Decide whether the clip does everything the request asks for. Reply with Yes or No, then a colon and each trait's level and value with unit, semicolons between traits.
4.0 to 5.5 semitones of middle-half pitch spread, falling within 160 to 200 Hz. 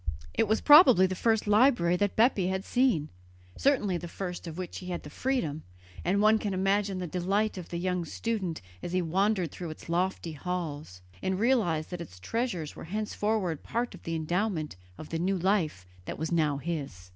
Yes: average, 4.3 semitones; medium, 185 Hz